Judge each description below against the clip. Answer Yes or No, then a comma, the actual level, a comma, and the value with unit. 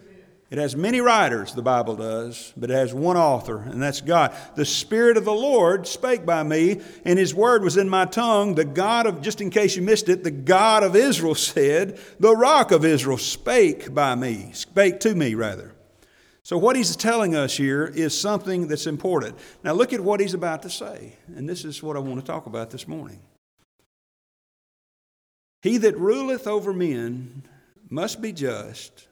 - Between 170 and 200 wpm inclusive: Yes, average, 190 wpm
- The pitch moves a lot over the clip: Yes, wide, 6.8 semitones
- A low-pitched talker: No, medium, 175 Hz